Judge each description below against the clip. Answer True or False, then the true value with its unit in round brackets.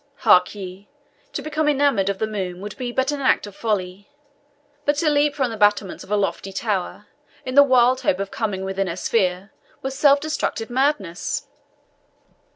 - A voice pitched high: True (215 Hz)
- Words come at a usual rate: True (180 wpm)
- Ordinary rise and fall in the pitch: False (5.9 semitones)